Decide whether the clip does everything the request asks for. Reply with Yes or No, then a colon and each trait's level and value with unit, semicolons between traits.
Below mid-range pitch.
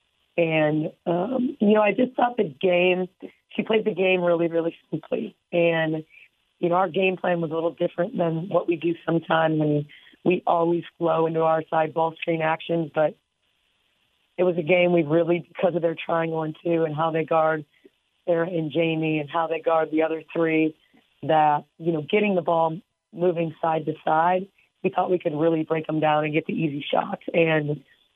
No: medium, 165 Hz